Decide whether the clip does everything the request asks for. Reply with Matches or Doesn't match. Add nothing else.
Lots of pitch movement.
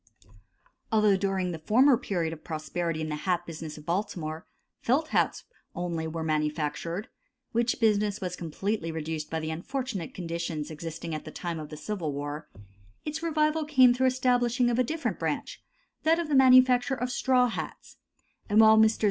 Matches